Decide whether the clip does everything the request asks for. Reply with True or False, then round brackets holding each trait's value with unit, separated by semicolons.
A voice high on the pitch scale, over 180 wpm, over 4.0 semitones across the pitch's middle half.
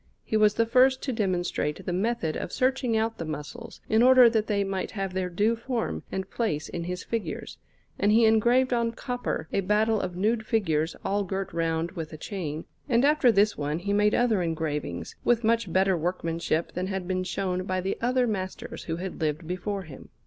True (195 Hz; 200 wpm; 4.6 semitones)